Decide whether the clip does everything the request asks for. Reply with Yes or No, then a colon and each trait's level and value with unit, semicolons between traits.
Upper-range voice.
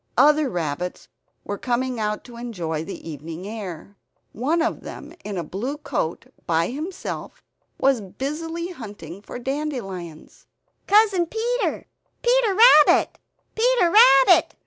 Yes: high, 245 Hz